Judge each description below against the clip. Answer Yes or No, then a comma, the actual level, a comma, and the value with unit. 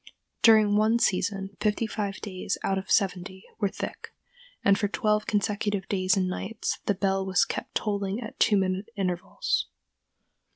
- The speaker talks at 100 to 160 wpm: Yes, average, 155 wpm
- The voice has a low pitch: No, high, 200 Hz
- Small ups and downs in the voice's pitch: Yes, narrow, 1.8 semitones